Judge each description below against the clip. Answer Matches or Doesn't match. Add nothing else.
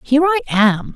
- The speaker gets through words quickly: Doesn't match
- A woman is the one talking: Matches